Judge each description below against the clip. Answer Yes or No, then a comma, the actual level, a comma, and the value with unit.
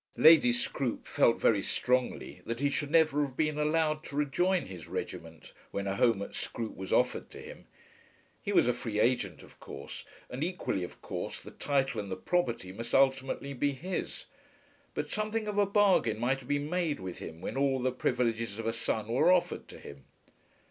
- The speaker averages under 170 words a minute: No, average, 195 wpm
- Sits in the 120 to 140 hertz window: Yes, low, 135 Hz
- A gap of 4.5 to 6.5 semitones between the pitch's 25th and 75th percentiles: Yes, wide, 5.6 semitones